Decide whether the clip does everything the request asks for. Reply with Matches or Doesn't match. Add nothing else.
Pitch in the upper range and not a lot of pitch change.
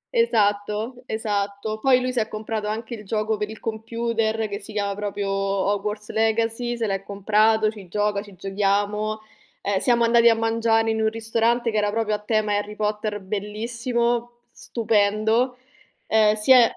Matches